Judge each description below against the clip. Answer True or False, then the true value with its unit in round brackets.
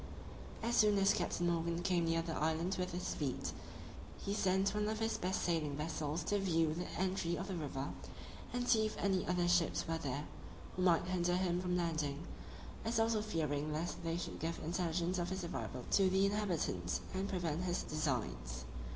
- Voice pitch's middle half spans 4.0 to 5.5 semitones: False (3.0 semitones)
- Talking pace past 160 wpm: True (185 wpm)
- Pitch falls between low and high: True (175 Hz)